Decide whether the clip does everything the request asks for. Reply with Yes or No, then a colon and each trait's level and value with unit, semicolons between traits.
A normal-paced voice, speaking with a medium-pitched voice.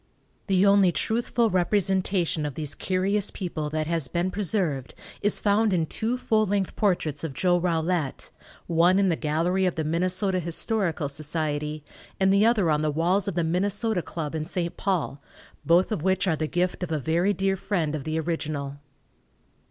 Yes: average, 175 wpm; medium, 175 Hz